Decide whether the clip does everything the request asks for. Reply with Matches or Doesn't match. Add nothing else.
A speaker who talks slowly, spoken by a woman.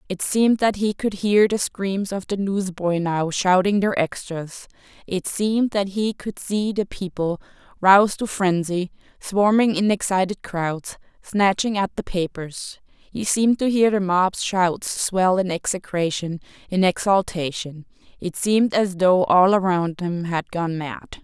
Doesn't match